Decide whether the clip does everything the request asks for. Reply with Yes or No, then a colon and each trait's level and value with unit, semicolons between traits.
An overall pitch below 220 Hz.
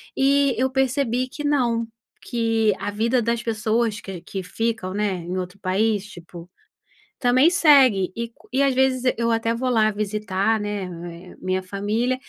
No: high, 225 Hz